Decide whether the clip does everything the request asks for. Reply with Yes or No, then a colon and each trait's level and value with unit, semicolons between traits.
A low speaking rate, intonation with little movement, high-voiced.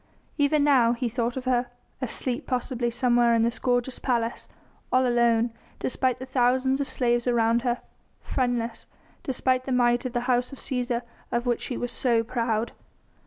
No: average, 165 wpm; narrow, 1.3 semitones; high, 245 Hz